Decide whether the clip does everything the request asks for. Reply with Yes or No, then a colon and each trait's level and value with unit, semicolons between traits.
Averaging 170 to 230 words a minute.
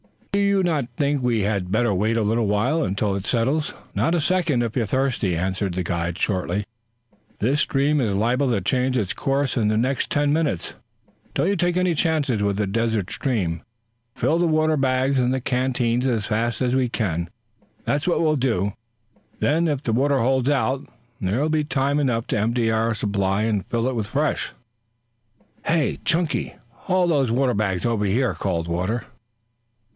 Yes: average, 185 wpm